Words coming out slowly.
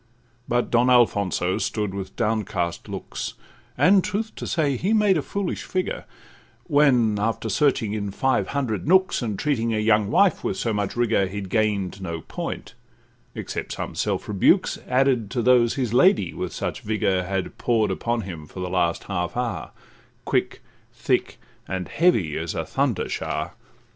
No: average, 160 wpm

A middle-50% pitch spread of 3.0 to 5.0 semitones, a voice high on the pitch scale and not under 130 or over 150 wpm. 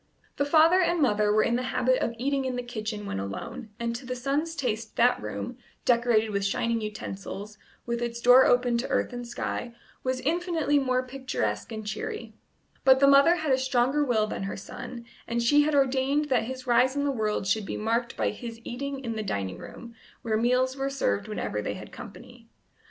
No: average, 3.5 semitones; high, 245 Hz; fast, 205 wpm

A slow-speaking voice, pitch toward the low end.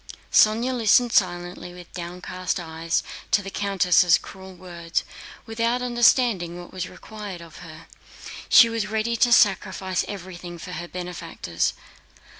No: slow, 130 wpm; medium, 185 Hz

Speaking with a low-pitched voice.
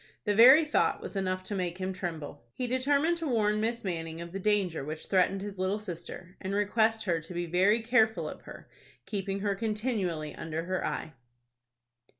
No: high, 195 Hz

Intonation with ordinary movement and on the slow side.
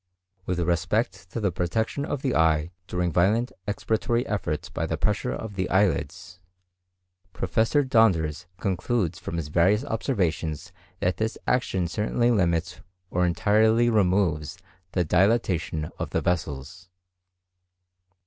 Yes: average, 4.5 semitones; slow, 125 wpm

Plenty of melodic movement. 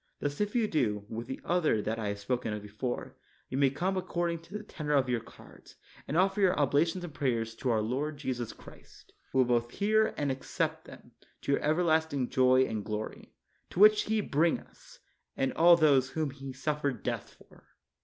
Yes: wide, 5.7 semitones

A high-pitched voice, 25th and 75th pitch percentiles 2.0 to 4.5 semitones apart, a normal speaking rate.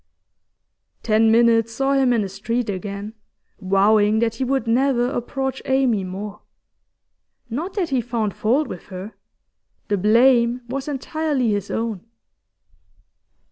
No: high, 230 Hz; average, 4.0 semitones; slow, 130 wpm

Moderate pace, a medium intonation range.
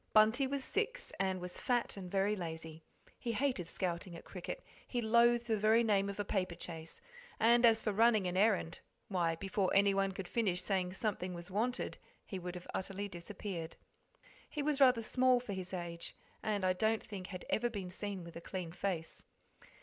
Yes: average, 190 wpm; average, 3.8 semitones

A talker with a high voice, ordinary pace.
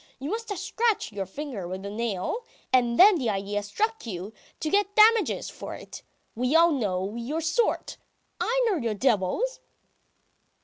Yes: very high, 260 Hz; average, 165 wpm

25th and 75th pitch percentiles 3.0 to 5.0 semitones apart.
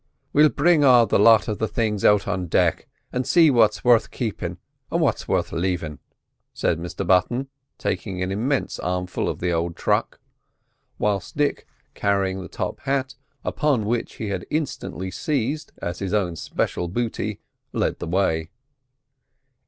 No: wide, 5.5 semitones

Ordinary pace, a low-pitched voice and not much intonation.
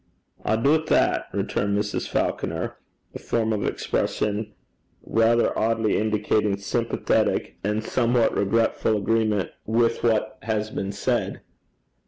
No: slow, 115 wpm; low, 110 Hz; narrow, 1.6 semitones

